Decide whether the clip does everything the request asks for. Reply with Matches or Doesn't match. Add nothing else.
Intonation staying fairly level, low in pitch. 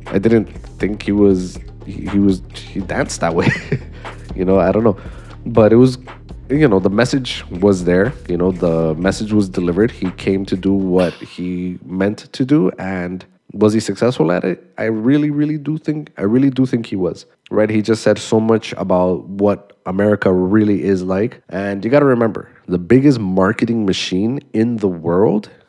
Doesn't match